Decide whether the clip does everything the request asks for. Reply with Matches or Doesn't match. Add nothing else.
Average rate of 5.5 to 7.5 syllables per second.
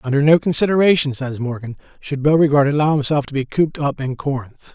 Matches